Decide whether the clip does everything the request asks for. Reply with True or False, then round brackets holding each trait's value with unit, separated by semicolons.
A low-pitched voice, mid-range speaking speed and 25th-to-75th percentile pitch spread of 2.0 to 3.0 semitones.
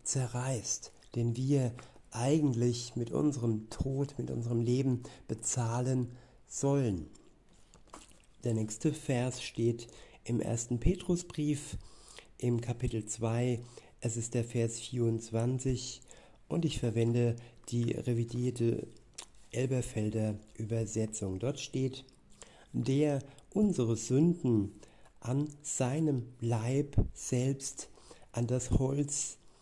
False (125 Hz; 95 wpm; 2.7 semitones)